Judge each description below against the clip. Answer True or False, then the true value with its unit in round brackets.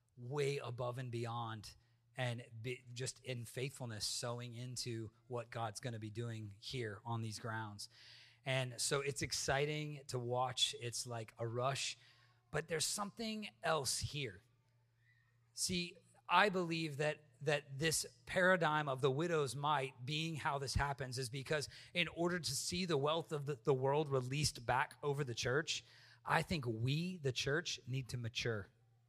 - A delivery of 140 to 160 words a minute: True (155 wpm)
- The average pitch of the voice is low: True (130 Hz)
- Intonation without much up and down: False (3.8 semitones)